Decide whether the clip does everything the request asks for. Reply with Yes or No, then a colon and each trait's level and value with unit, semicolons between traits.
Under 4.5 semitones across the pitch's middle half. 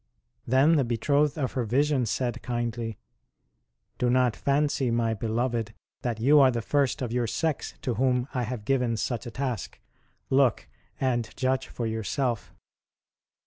Yes: narrow, 2.6 semitones